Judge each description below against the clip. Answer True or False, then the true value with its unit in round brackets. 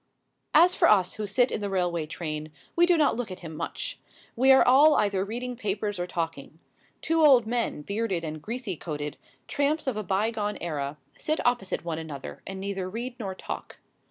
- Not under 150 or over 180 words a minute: False (190 wpm)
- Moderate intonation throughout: False (6.2 semitones)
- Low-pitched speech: False (205 Hz)